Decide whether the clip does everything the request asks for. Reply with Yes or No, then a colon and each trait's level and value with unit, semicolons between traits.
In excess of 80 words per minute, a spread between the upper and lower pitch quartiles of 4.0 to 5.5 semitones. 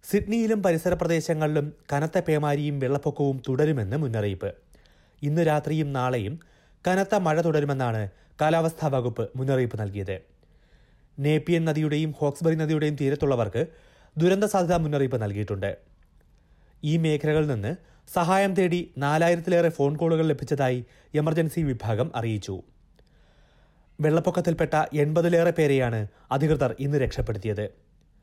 Yes: average, 95 wpm; average, 4.4 semitones